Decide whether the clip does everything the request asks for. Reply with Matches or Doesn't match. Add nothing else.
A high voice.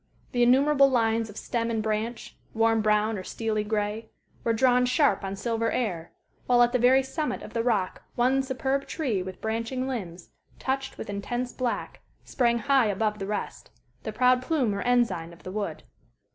Matches